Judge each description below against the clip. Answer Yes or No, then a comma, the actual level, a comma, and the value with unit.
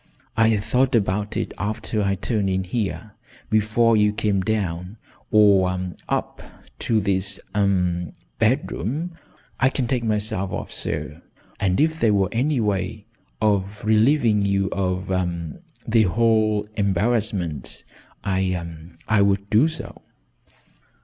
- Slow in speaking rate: Yes, slow, 125 wpm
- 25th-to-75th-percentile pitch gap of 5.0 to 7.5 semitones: No, average, 2.7 semitones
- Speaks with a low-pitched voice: Yes, low, 105 Hz